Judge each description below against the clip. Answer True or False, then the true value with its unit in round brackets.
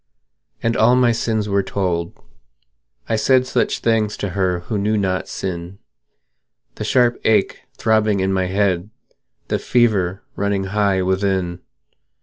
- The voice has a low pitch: True (100 Hz)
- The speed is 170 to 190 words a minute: False (135 wpm)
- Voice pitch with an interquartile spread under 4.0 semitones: True (2.8 semitones)